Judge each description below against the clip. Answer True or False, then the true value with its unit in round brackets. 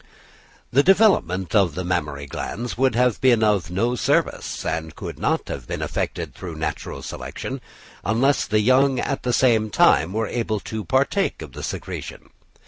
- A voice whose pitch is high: False (110 Hz)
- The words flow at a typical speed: True (165 wpm)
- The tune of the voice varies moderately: False (5.9 semitones)